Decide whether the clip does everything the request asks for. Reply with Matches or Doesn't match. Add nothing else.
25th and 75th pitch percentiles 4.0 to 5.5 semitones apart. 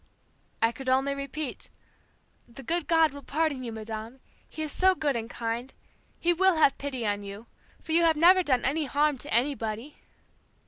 Matches